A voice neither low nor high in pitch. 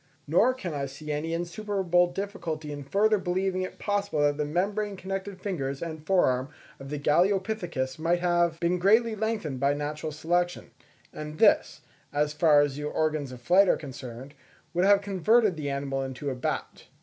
Yes: medium, 170 Hz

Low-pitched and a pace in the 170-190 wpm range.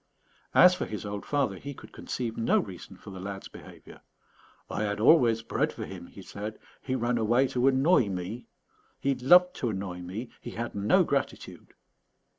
Yes: low, 115 Hz; average, 180 wpm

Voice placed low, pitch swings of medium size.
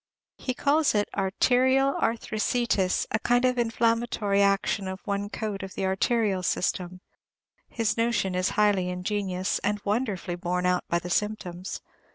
No: high, 205 Hz; average, 3.6 semitones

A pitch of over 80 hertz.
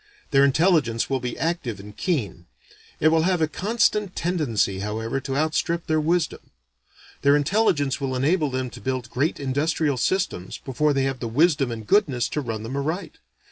Yes: medium, 140 Hz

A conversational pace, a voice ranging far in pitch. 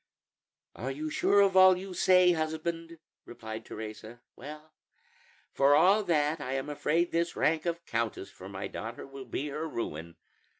Yes: average, 160 wpm; wide, 6.1 semitones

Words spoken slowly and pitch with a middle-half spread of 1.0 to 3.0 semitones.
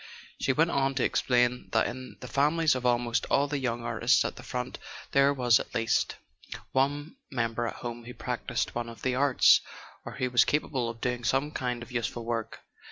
No: average, 200 wpm; narrow, 2.4 semitones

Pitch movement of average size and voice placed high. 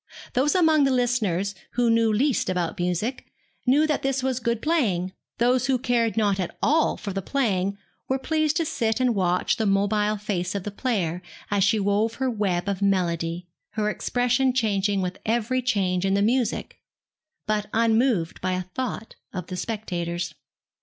Yes: average, 4.7 semitones; high, 215 Hz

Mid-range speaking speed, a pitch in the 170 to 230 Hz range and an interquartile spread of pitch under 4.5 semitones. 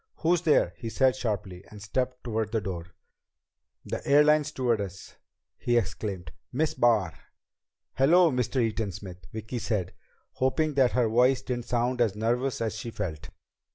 No: average, 150 wpm; low, 120 Hz; average, 4.1 semitones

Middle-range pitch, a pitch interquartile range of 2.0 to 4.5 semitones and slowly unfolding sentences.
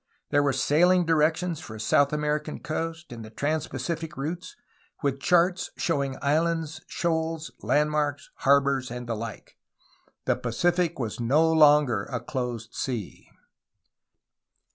Yes: medium, 150 Hz; average, 4.0 semitones; slow, 130 wpm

